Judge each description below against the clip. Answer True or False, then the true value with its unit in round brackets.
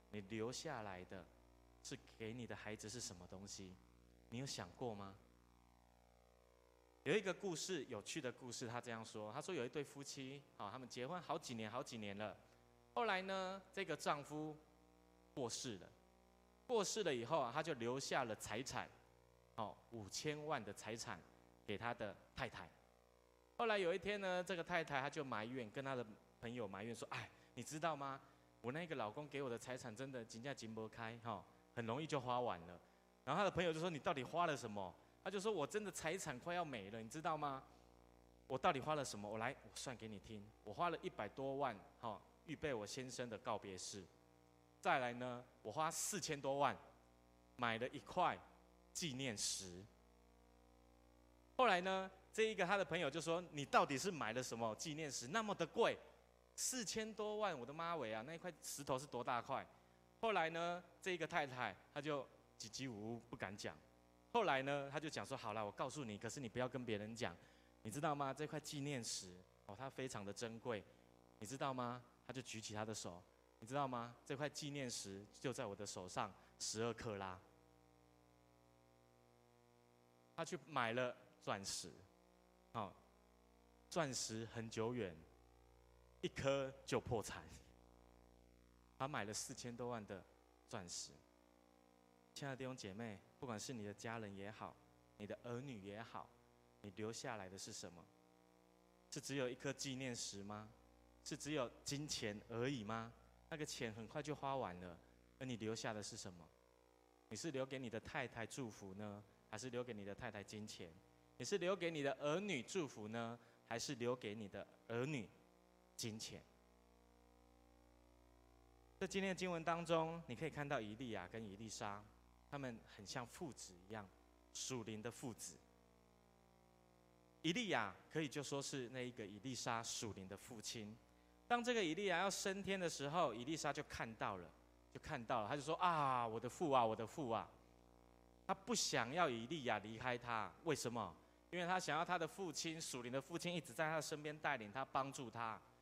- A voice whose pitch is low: True (110 Hz)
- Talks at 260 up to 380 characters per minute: False (250 characters per minute)